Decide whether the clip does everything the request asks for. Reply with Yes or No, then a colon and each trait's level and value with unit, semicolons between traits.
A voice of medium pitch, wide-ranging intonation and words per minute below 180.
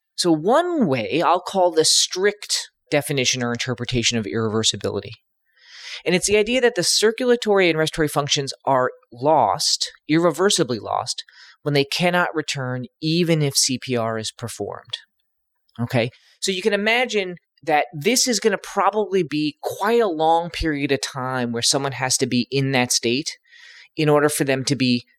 Yes: medium, 150 Hz; wide, 7.3 semitones; average, 160 wpm